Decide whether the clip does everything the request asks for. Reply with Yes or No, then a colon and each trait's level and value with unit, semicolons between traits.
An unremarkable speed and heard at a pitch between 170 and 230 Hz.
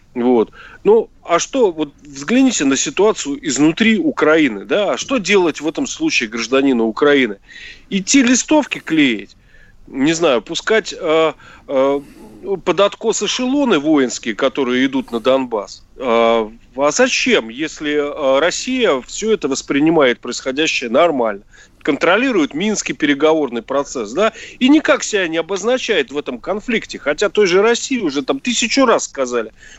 Yes: average, 135 wpm; high, 190 Hz